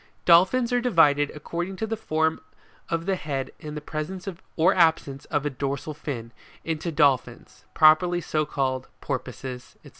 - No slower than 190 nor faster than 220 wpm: No, average, 155 wpm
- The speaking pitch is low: No, medium, 155 Hz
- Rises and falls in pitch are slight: No, average, 3.7 semitones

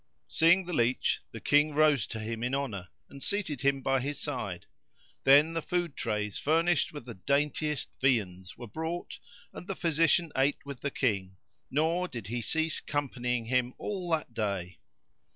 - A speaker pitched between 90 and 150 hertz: Yes, medium, 140 Hz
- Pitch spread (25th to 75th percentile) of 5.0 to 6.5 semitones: Yes, average, 5.3 semitones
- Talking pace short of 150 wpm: No, average, 170 wpm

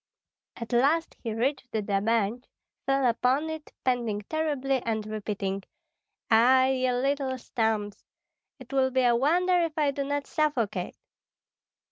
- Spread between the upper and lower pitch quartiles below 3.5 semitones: No, average, 4.0 semitones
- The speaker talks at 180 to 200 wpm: No, slow, 135 wpm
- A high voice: Yes, very high, 255 Hz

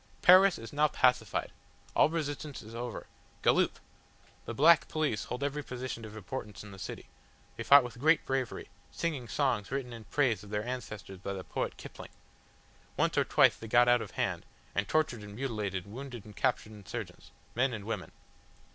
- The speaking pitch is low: Yes, low, 120 Hz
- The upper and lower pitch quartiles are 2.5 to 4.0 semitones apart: No, average, 4.6 semitones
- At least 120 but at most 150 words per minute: No, average, 180 wpm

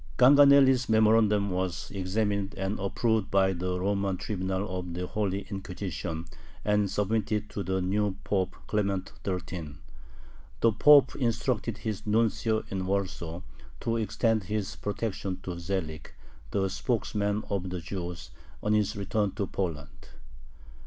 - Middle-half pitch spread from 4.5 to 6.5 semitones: No, narrow, 2.5 semitones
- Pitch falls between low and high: No, low, 100 Hz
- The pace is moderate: No, slow, 130 wpm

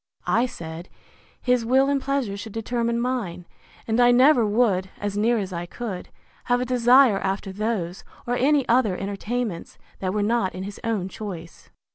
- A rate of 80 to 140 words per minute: No, average, 170 wpm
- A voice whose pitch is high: Yes, high, 225 Hz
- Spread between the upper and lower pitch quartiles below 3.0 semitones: No, average, 4.3 semitones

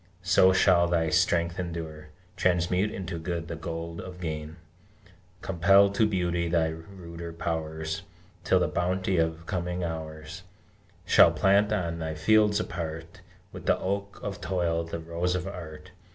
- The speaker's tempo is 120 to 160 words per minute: Yes, average, 145 wpm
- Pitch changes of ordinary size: No, narrow, 2.1 semitones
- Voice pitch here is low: Yes, very low, 85 Hz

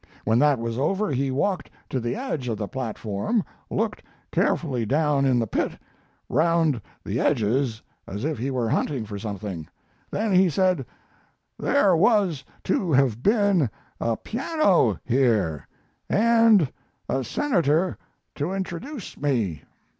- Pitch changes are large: Yes, wide, 8.2 semitones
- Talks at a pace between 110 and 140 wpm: Yes, slow, 135 wpm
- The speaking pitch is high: No, medium, 140 Hz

